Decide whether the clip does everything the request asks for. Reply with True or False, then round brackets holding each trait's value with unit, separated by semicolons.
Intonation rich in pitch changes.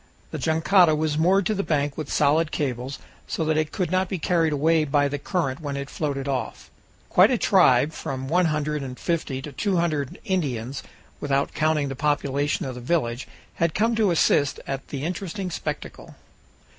False (3.4 semitones)